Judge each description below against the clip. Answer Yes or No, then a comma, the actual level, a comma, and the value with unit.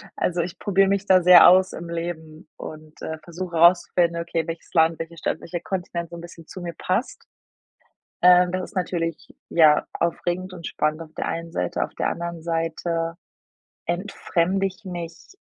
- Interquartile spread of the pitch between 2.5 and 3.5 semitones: No, narrow, 1.6 semitones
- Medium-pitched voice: Yes, medium, 170 Hz